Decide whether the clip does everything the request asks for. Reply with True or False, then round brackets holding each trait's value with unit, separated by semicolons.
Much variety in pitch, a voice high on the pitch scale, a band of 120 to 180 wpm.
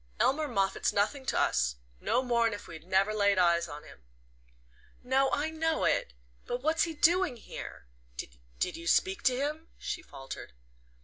True (8.5 semitones; 245 Hz; 165 wpm)